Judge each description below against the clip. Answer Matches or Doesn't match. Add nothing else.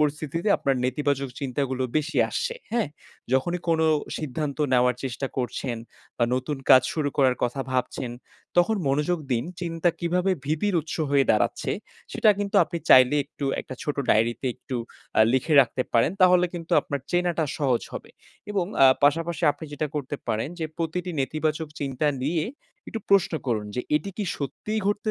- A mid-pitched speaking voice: Matches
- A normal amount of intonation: Matches